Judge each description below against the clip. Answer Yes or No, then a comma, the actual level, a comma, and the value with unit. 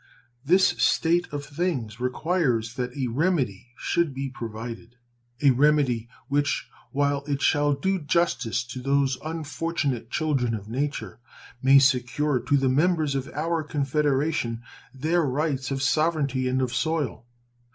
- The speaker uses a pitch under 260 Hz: Yes, medium, 140 Hz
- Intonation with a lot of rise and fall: No, average, 3.5 semitones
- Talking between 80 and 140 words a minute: Yes, slow, 135 wpm